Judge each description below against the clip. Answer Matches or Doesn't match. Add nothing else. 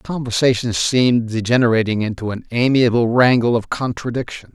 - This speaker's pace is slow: Matches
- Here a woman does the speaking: Doesn't match